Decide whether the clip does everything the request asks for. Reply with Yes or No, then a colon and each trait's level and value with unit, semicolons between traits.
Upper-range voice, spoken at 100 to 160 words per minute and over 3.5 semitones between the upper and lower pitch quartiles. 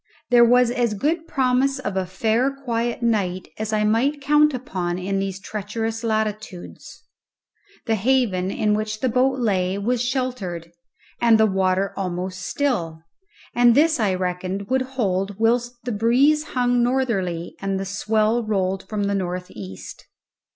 Yes: high, 220 Hz; average, 150 wpm; average, 4.6 semitones